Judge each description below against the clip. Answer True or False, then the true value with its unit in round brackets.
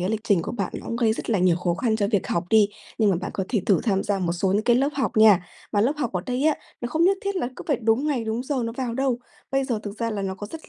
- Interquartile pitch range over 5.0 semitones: False (4.3 semitones)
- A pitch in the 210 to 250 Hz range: True (220 Hz)